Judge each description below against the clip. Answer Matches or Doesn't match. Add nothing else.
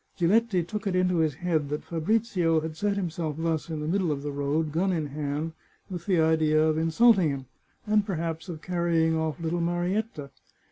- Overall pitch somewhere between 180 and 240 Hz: Doesn't match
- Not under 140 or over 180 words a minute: Doesn't match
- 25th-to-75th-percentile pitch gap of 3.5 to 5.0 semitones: Doesn't match